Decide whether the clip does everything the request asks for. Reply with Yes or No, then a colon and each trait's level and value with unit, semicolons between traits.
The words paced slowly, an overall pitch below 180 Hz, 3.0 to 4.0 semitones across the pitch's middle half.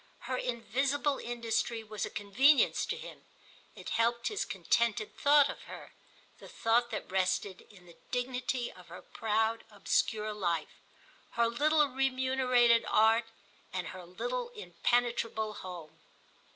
No: slow, 130 wpm; high, 230 Hz; average, 3.6 semitones